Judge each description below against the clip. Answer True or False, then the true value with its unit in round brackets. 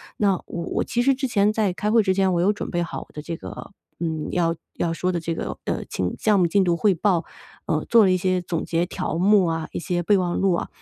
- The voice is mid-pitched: True (180 Hz)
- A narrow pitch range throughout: False (3.1 semitones)